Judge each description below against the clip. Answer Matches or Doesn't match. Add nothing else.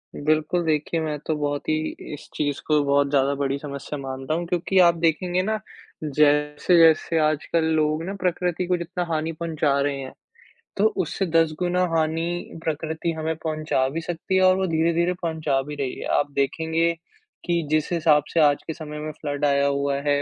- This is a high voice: Doesn't match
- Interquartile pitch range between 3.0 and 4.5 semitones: Doesn't match